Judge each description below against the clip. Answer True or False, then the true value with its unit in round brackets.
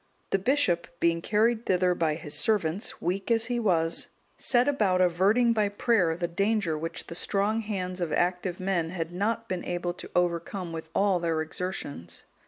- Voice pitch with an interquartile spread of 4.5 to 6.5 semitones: False (3.8 semitones)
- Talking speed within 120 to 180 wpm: True (175 wpm)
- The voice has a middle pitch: True (180 Hz)